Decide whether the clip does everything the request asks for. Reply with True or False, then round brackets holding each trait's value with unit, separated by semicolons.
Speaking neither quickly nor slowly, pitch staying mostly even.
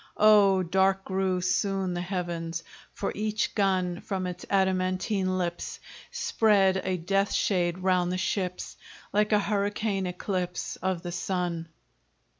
False (130 wpm; 1.7 semitones)